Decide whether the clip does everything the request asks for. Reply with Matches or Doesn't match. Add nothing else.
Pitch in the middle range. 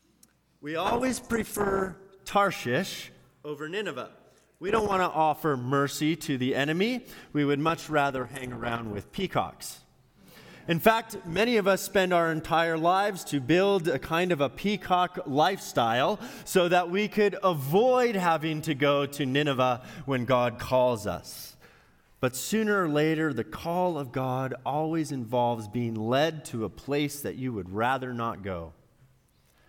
Matches